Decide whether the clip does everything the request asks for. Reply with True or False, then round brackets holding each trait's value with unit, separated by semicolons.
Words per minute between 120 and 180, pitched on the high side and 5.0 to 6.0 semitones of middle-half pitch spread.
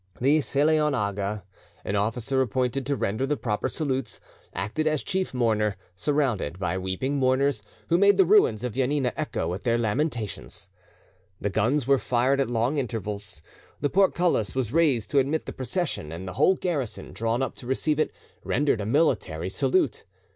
False (170 wpm; 130 Hz; 5.3 semitones)